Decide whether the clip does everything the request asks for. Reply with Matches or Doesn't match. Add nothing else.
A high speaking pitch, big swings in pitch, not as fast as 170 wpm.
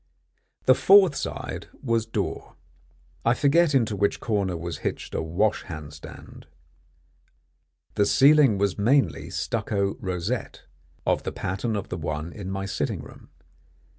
Doesn't match